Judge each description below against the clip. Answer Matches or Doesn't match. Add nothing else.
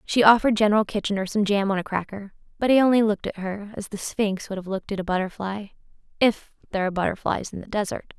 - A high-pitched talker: Matches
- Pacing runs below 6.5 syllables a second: Doesn't match